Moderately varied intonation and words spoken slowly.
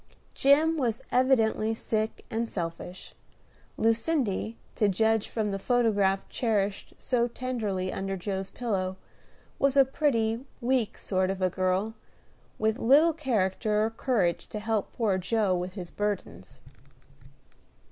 Yes: average, 3.9 semitones; slow, 125 wpm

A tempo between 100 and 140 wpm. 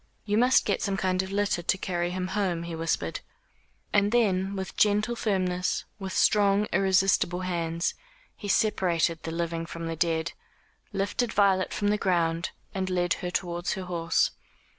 No: average, 160 wpm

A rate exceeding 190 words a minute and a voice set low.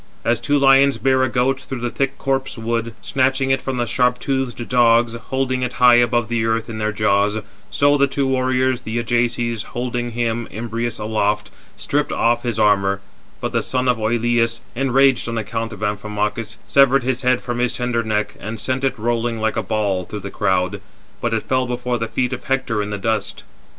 Yes: average, 200 wpm; low, 120 Hz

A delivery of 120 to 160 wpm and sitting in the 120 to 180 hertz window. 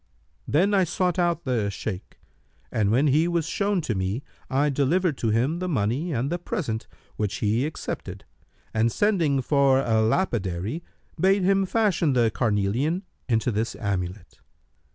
Yes: average, 155 wpm; low, 135 Hz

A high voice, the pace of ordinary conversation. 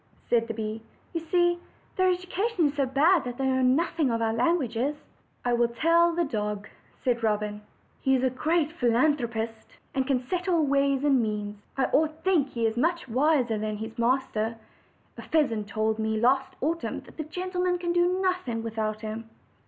Yes: very high, 265 Hz; average, 185 wpm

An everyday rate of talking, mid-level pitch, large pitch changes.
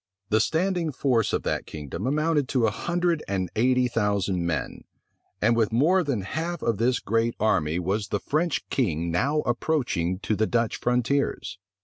No: average, 165 wpm; low, 115 Hz; wide, 6.5 semitones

